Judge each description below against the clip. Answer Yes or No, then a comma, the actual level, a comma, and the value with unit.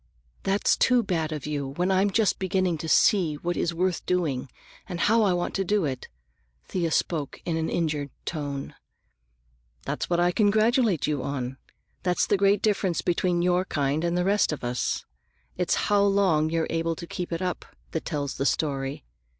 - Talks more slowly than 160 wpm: No, average, 180 wpm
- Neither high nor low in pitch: Yes, medium, 175 Hz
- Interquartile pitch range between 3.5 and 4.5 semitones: Yes, average, 3.9 semitones